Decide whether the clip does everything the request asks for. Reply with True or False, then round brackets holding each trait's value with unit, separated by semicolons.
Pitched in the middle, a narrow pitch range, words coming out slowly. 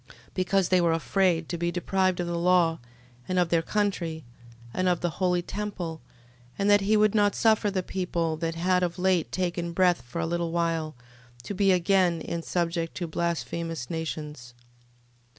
False (175 Hz; 2.1 semitones; 175 wpm)